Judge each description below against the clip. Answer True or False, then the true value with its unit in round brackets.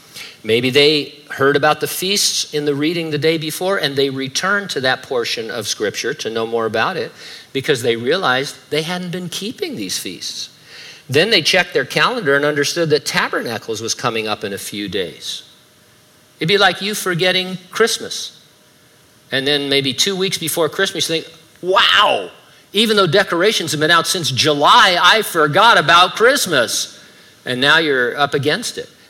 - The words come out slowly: False (175 wpm)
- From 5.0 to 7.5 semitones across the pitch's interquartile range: True (5.4 semitones)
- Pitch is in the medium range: True (160 Hz)